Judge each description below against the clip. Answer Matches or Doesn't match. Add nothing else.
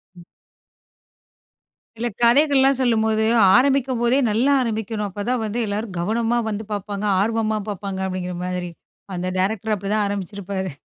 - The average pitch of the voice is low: Doesn't match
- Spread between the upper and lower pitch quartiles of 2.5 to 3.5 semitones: Matches